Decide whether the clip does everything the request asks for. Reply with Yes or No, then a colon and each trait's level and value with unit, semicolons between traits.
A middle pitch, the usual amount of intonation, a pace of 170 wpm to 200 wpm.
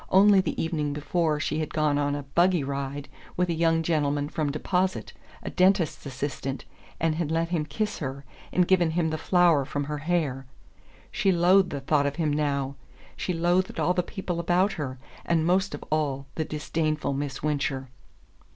Yes: medium, 155 Hz; average, 3.5 semitones; average, 180 wpm